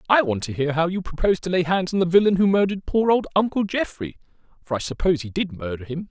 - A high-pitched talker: No, medium, 175 Hz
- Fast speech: Yes, fast, 245 wpm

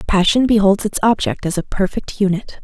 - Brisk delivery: No, average, 180 wpm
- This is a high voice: Yes, high, 205 Hz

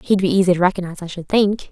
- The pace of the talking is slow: No, fast, 280 wpm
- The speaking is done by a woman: Yes, female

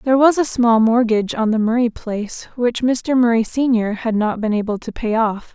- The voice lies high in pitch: Yes, high, 230 Hz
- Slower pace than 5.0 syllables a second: No, 5.2 syllables/s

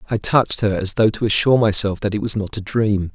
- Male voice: Yes, male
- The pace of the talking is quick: Yes, fast, 265 wpm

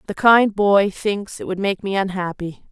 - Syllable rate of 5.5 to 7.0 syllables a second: No, 4.4 syllables/s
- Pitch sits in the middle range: No, high, 195 Hz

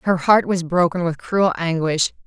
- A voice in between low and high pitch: Yes, medium, 175 Hz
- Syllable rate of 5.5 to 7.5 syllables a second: No, 4.5 syllables/s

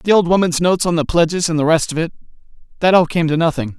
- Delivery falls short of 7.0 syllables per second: No, 7.1 syllables/s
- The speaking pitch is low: No, medium, 165 Hz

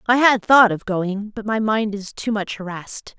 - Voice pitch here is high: Yes, high, 210 Hz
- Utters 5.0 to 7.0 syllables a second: No, 4.6 syllables/s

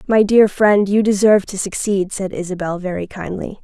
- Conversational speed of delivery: Yes, average, 180 wpm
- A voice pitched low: No, high, 195 Hz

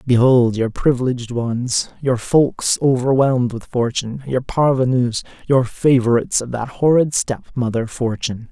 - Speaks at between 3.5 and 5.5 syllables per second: Yes, 4.7 syllables/s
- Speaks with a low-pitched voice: Yes, low, 125 Hz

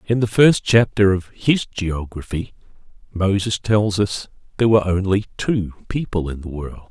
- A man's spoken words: Yes, male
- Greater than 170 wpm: No, average, 155 wpm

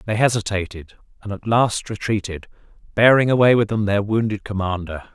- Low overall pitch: Yes, low, 105 Hz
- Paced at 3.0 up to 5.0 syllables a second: No, 5.4 syllables/s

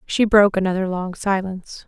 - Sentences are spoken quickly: No, average, 160 wpm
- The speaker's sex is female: Yes, female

